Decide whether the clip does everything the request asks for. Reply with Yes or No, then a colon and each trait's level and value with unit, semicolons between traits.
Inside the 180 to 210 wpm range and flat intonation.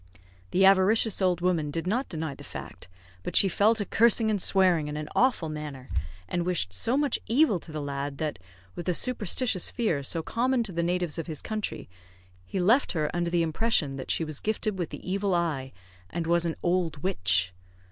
No: average, 200 wpm; average, 5.1 semitones